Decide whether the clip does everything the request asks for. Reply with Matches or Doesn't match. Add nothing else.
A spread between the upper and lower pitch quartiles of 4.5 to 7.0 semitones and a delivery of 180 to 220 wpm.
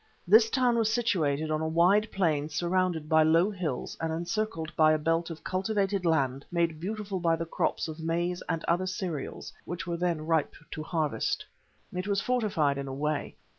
Doesn't match